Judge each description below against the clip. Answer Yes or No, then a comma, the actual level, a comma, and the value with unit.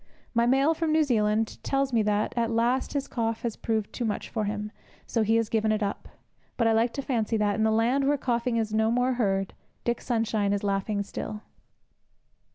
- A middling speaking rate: No, fast, 210 wpm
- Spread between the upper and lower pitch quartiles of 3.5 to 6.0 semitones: No, narrow, 2.5 semitones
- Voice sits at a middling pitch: No, high, 225 Hz